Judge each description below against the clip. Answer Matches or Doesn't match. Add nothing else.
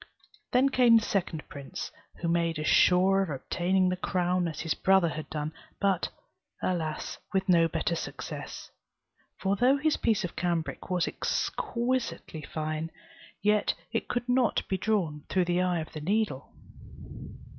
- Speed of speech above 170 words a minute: Doesn't match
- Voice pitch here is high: Doesn't match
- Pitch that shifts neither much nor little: Matches